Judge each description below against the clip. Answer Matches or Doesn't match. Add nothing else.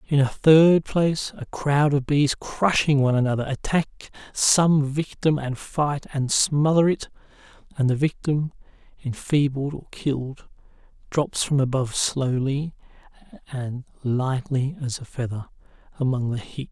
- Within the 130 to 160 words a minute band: Matches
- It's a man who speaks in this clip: Matches